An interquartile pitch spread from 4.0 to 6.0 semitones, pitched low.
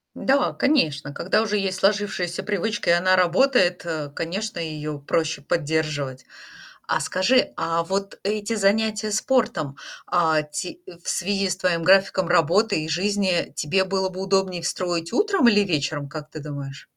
No: average, 4.3 semitones; medium, 180 Hz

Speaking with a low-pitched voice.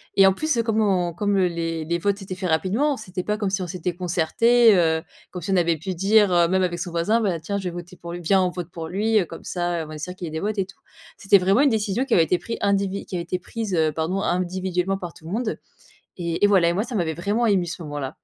No: medium, 185 Hz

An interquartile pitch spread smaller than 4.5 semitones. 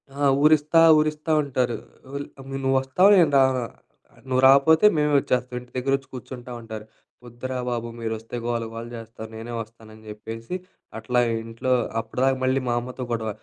Yes: average, 2.9 semitones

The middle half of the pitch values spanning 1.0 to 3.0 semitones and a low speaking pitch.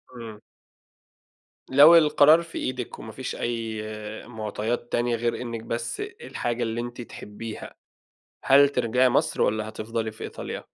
Yes: narrow, 2.5 semitones; low, 120 Hz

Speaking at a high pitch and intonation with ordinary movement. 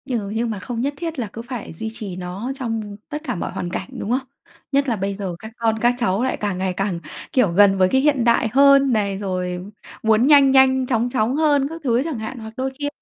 Yes: high, 230 Hz; average, 4.7 semitones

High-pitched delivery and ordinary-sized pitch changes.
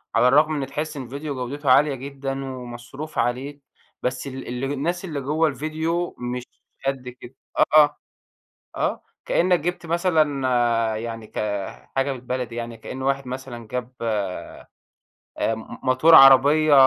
No: low, 135 Hz; average, 3.2 semitones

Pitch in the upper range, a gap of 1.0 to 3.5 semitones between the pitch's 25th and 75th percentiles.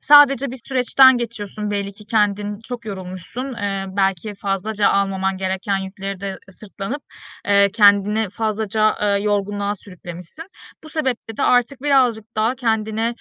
Yes: high, 210 Hz; average, 2.9 semitones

